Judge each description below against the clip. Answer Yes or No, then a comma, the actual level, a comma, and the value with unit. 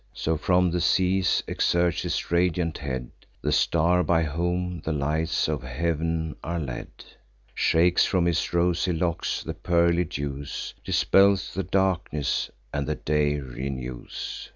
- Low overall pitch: Yes, very low, 85 Hz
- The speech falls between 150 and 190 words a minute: No, slow, 135 wpm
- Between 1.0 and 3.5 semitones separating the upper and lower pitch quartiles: Yes, average, 3.2 semitones